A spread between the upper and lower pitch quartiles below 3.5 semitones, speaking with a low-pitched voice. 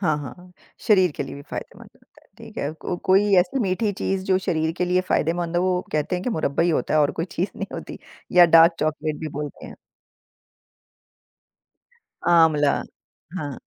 No: average, 3.1 semitones; medium, 170 Hz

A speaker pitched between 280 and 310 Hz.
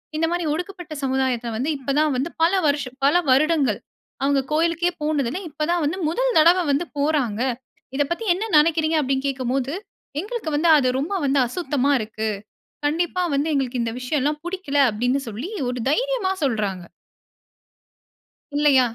Yes: very high, 290 Hz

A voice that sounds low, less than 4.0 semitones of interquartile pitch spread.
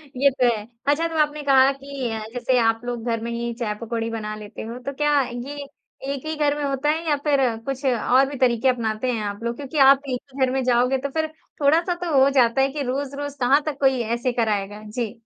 No: very high, 260 Hz; average, 3.2 semitones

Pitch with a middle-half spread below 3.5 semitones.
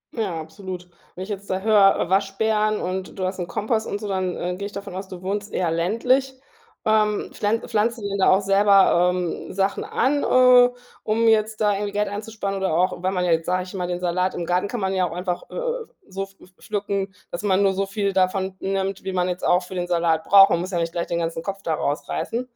Yes: narrow, 2.4 semitones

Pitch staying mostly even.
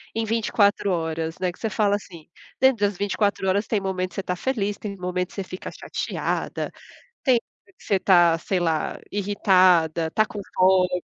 Yes: narrow, 2.3 semitones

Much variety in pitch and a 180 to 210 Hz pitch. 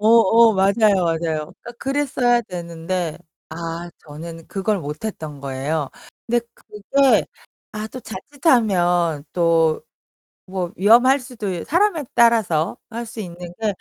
Yes: wide, 6.0 semitones; medium, 185 Hz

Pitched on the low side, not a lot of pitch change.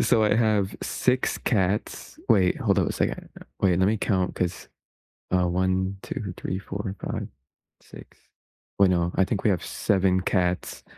Yes: very low, 95 Hz; narrow, 2.1 semitones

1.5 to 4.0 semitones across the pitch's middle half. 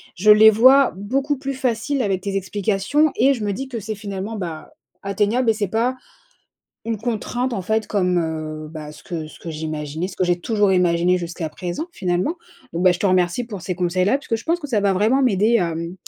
No: average, 4.7 semitones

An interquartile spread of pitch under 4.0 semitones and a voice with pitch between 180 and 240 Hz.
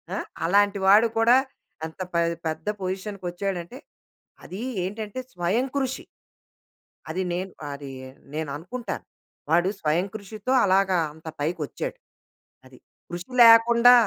No: average, 4.3 semitones; high, 190 Hz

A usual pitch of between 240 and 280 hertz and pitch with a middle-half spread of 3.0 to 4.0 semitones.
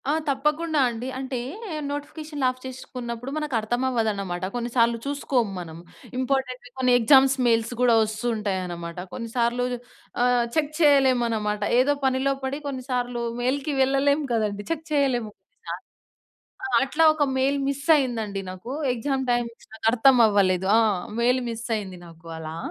Yes: high, 245 Hz; average, 3.5 semitones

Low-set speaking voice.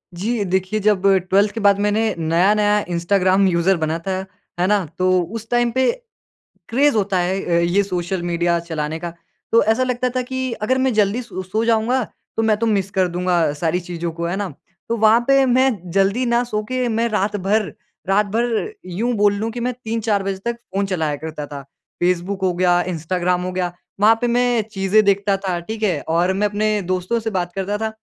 No: high, 200 Hz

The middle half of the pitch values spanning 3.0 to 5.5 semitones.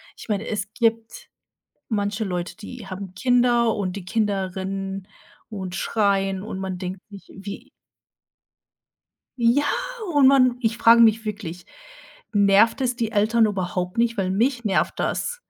Yes: average, 3.3 semitones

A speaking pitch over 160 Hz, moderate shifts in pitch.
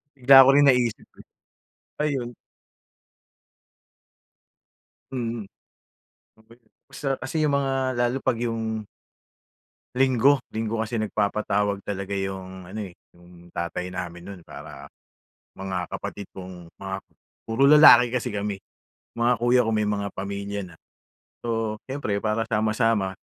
No: low, 110 Hz; average, 3.9 semitones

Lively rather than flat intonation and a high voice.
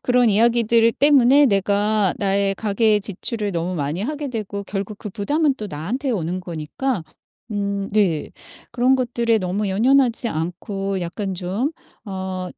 No: average, 4.0 semitones; high, 205 Hz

